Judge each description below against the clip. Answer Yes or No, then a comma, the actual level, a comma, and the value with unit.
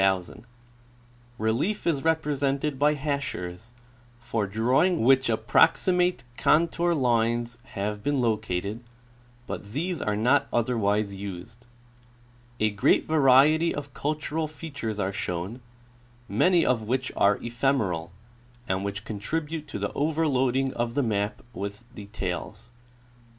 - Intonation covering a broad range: Yes, wide, 5.8 semitones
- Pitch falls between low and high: No, low, 120 Hz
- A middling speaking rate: No, slow, 115 wpm